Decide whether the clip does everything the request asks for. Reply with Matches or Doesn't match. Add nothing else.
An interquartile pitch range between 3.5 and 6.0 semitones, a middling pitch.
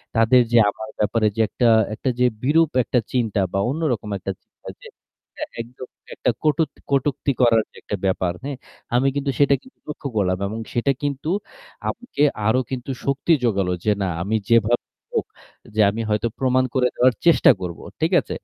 Doesn't match